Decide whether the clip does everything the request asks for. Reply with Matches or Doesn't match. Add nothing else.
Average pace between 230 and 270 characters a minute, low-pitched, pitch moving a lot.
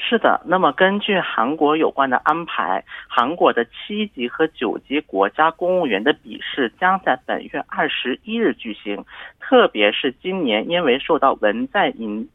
Doesn't match